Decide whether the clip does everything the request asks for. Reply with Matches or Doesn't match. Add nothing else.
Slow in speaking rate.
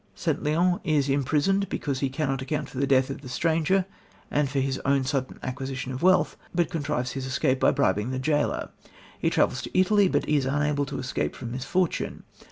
Doesn't match